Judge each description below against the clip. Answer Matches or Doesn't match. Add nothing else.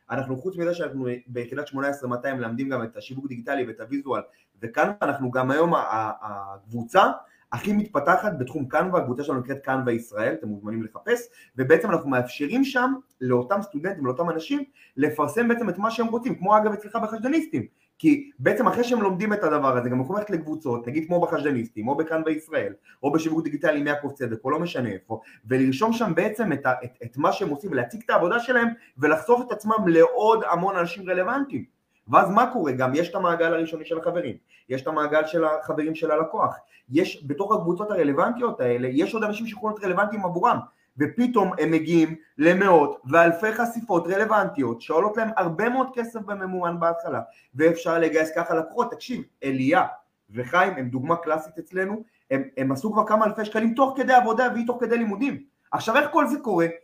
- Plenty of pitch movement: Matches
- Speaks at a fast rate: Matches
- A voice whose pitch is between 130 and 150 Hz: Doesn't match